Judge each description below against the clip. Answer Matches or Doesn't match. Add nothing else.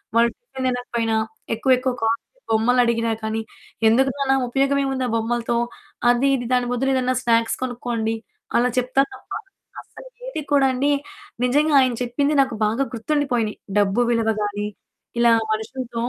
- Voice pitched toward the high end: Matches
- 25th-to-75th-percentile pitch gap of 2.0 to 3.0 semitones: Matches